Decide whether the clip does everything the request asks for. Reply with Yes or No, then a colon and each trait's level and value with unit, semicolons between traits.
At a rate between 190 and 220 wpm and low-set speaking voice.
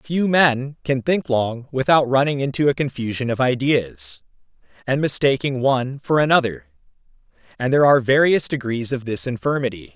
No: average, 150 wpm; low, 130 Hz